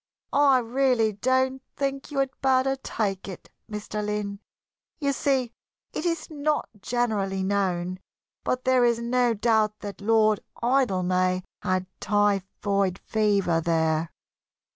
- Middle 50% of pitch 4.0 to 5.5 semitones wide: Yes, average, 4.9 semitones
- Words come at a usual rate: No, slow, 120 wpm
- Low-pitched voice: No, high, 215 Hz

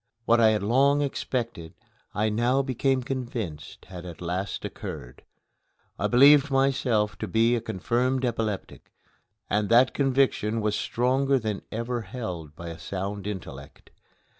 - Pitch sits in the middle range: No, low, 115 Hz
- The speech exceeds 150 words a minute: No, average, 140 wpm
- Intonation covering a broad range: No, average, 4.3 semitones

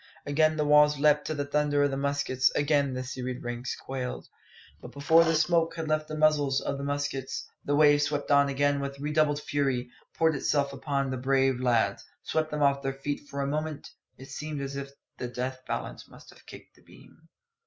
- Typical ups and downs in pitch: No, narrow, 1.7 semitones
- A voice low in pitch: No, medium, 145 Hz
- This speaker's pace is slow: No, fast, 205 wpm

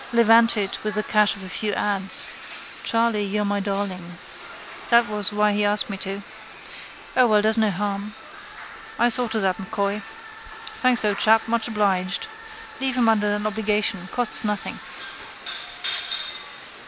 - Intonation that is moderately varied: No, narrow, 1.9 semitones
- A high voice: Yes, high, 210 Hz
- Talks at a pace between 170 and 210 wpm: No, average, 145 wpm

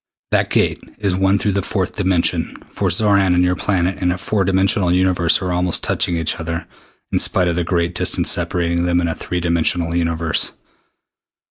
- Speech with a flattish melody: Yes, narrow, 1.9 semitones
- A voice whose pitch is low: Yes, very low, 90 Hz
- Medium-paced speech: Yes, average, 195 wpm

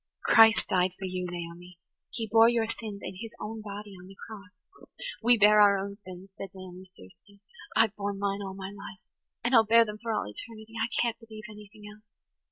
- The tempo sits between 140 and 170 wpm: No, average, 195 wpm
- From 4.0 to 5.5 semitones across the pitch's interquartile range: No, narrow, 2.6 semitones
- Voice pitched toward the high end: Yes, high, 205 Hz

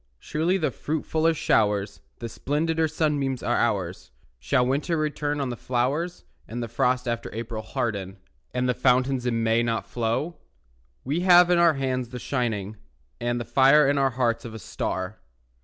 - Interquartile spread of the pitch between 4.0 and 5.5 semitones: Yes, average, 4.4 semitones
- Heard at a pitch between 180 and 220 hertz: No, low, 125 Hz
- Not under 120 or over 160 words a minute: No, average, 170 wpm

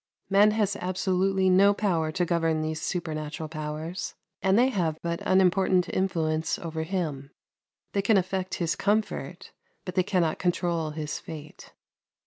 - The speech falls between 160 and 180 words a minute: No, average, 140 wpm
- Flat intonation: No, average, 3.2 semitones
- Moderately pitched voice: Yes, medium, 180 Hz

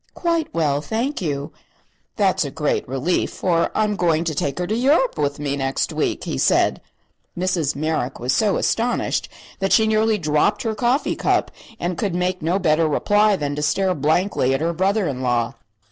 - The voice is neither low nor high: Yes, medium, 175 Hz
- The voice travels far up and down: Yes, wide, 6.1 semitones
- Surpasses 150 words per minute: Yes, average, 185 wpm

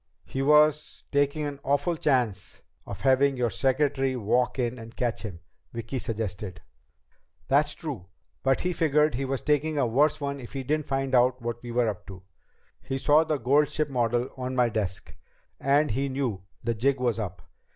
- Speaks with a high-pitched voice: No, low, 130 Hz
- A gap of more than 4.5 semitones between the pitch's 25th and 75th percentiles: No, average, 3.4 semitones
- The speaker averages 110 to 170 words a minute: No, average, 180 wpm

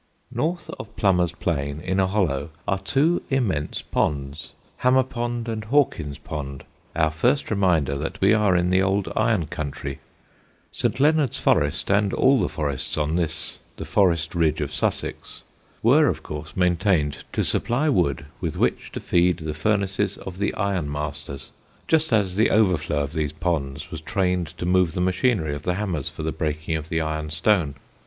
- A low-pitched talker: Yes, very low, 90 Hz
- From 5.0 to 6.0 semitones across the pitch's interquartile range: Yes, wide, 5.4 semitones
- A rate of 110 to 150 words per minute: No, average, 175 wpm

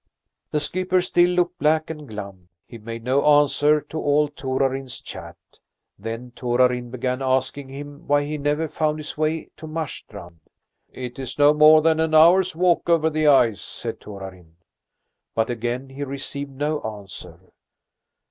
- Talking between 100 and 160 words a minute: Yes, average, 155 wpm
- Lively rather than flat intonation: No, average, 4.1 semitones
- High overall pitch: No, medium, 140 Hz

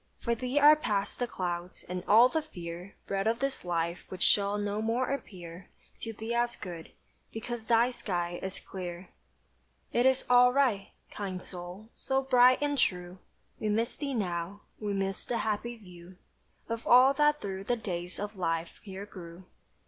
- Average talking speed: Yes, average, 170 wpm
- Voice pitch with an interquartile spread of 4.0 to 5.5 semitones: Yes, average, 5.1 semitones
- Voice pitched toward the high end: Yes, high, 205 Hz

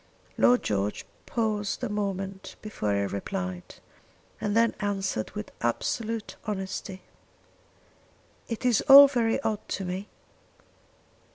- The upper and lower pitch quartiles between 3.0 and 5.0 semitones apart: Yes, average, 3.9 semitones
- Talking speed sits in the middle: No, slow, 110 wpm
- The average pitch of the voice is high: Yes, high, 205 Hz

